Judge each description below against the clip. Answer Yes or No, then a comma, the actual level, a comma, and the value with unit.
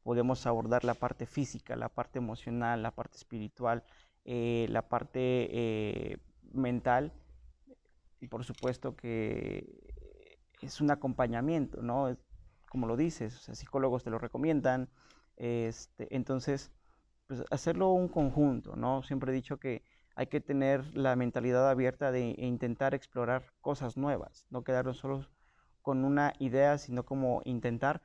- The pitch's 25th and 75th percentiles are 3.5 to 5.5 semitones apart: No, narrow, 2.5 semitones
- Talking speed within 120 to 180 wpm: Yes, average, 140 wpm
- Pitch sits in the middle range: No, low, 125 Hz